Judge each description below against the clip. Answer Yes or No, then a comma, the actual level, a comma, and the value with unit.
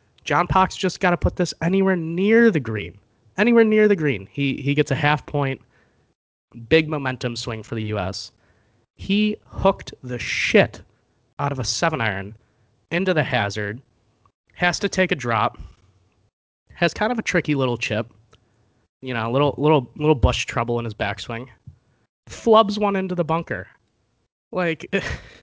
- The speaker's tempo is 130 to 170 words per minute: Yes, average, 160 wpm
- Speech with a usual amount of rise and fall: No, wide, 7.9 semitones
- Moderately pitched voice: No, low, 130 Hz